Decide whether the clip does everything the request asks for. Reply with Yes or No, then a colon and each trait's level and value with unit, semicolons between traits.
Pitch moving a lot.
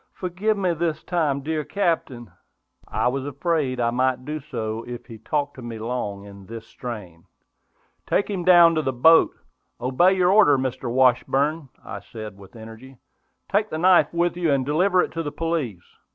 Yes: wide, 6.0 semitones